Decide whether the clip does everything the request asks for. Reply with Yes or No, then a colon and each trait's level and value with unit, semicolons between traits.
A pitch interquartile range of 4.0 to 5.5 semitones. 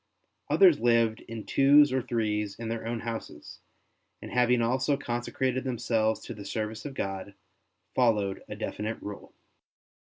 No: average, 2.8 semitones